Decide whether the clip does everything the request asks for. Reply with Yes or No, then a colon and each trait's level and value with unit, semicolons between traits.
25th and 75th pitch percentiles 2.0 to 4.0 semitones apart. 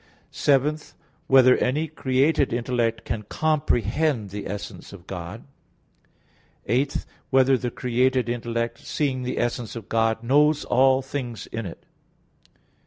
Yes: average, 2.9 semitones